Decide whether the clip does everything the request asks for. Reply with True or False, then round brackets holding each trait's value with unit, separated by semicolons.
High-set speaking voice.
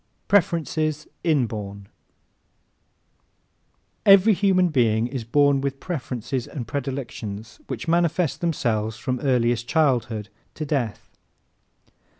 False (135 Hz)